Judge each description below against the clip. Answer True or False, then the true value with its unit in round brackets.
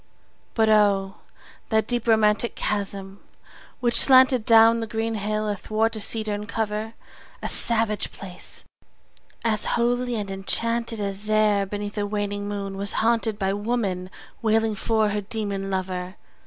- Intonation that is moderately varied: False (2.0 semitones)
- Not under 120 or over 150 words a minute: True (140 wpm)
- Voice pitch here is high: True (215 Hz)